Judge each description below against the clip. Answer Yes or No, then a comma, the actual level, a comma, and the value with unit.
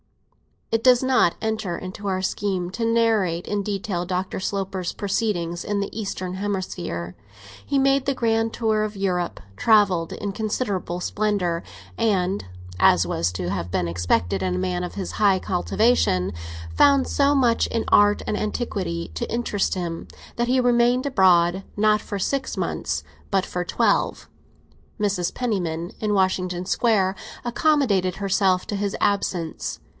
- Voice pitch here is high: Yes, high, 195 Hz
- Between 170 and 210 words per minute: No, average, 150 wpm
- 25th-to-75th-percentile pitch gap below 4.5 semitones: Yes, average, 3.9 semitones